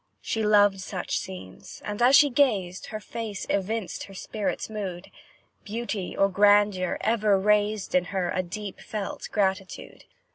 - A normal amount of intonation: No, narrow, 2.2 semitones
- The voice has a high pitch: Yes, high, 205 Hz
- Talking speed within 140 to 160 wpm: Yes, average, 145 wpm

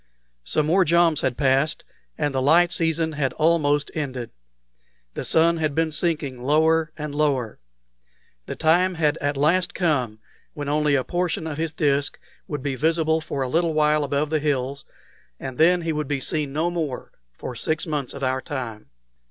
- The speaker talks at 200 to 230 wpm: No, average, 175 wpm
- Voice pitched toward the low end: No, medium, 150 Hz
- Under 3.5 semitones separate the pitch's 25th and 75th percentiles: Yes, narrow, 2.6 semitones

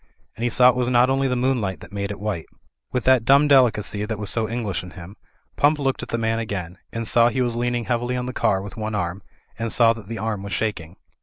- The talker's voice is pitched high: No, low, 115 Hz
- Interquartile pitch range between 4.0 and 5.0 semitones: No, average, 3.4 semitones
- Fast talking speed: Yes, fast, 255 wpm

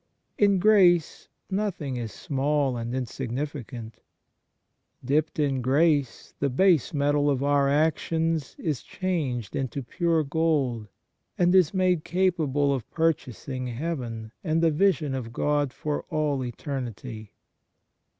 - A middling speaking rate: No, slow, 120 wpm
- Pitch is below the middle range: No, medium, 145 Hz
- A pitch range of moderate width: Yes, average, 4.2 semitones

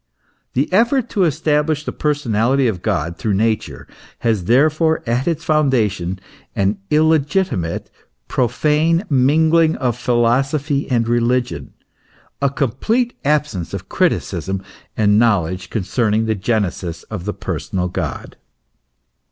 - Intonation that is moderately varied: No, wide, 6.5 semitones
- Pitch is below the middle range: Yes, low, 125 Hz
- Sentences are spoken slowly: Yes, slow, 115 wpm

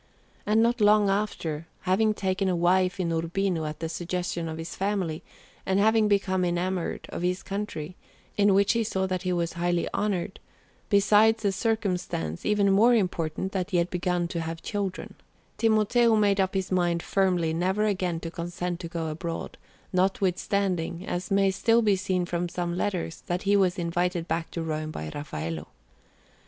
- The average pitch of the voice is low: No, medium, 185 Hz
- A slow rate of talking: No, average, 170 wpm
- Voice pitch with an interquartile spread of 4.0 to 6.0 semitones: No, average, 2.9 semitones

